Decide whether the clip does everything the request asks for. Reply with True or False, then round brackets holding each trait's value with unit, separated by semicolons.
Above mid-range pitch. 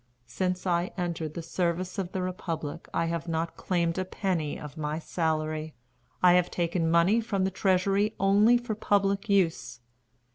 False (175 Hz)